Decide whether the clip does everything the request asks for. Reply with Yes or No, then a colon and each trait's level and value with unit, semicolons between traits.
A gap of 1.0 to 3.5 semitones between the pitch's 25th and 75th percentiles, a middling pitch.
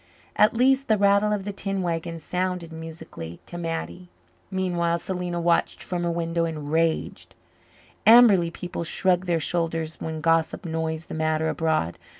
Yes: narrow, 2.4 semitones; medium, 170 Hz